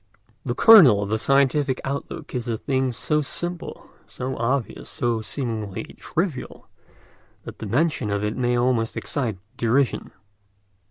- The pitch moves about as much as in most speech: Yes, average, 3.7 semitones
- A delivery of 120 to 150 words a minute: Yes, average, 140 wpm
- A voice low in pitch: Yes, low, 125 Hz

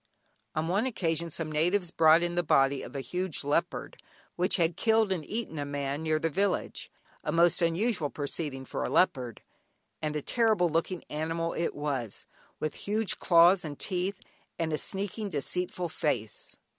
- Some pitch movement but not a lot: Yes, average, 3.4 semitones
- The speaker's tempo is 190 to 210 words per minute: No, average, 170 wpm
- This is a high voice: No, medium, 165 Hz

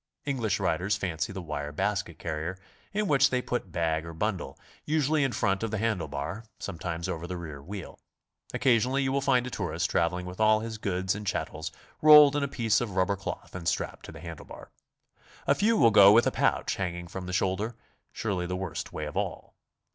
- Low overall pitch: Yes, very low, 95 Hz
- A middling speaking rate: No, fast, 210 wpm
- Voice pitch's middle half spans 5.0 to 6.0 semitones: Yes, wide, 5.5 semitones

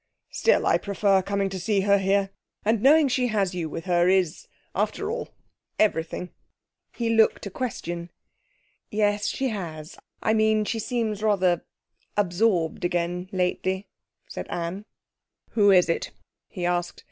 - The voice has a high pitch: Yes, high, 195 Hz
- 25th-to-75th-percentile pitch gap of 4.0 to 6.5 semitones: No, average, 3.5 semitones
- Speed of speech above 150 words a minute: No, average, 145 wpm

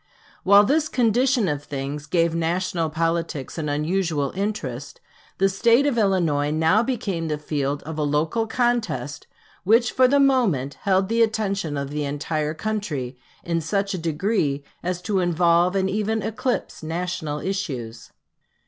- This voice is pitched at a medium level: Yes, medium, 175 Hz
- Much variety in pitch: Yes, wide, 6.0 semitones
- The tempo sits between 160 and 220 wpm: No, average, 150 wpm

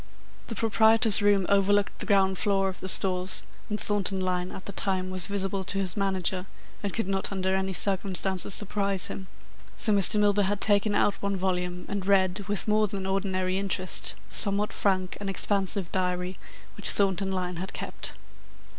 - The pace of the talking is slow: No, average, 175 wpm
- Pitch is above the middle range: Yes, high, 195 Hz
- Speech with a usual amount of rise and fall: No, narrow, 1.4 semitones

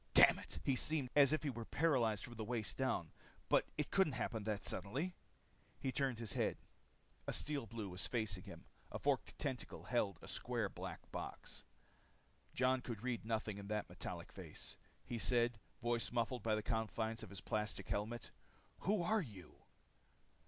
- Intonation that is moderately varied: Yes, average, 3.4 semitones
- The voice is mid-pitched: No, low, 115 Hz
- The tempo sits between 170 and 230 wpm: Yes, average, 175 wpm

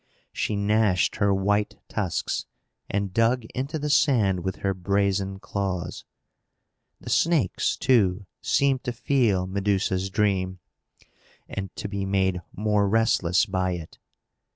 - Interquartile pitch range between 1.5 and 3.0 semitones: Yes, average, 2.7 semitones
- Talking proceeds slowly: Yes, slow, 125 wpm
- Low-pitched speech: Yes, low, 100 Hz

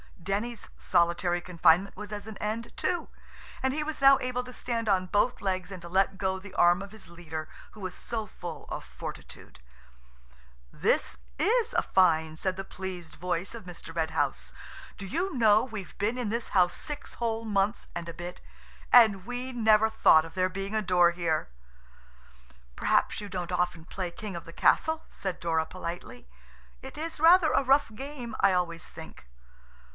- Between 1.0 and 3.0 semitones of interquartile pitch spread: No, average, 4.7 semitones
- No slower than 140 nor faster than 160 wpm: No, average, 180 wpm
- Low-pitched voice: No, high, 195 Hz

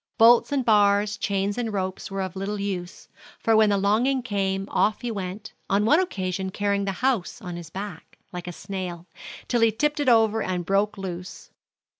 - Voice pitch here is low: No, high, 200 Hz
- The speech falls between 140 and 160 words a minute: No, average, 190 wpm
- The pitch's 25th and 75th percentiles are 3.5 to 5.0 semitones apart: No, average, 2.8 semitones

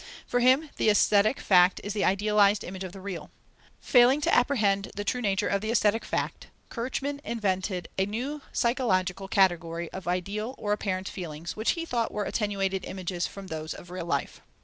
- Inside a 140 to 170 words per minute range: No, average, 180 wpm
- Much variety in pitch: No, average, 3.6 semitones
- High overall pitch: Yes, high, 200 Hz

